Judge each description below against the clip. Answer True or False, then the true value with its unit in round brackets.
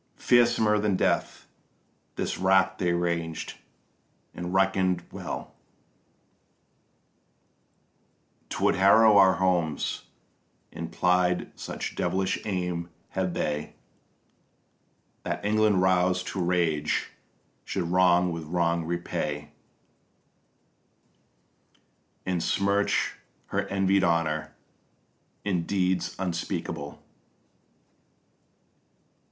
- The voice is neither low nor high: False (90 Hz)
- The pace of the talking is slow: True (80 wpm)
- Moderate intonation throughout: False (2.1 semitones)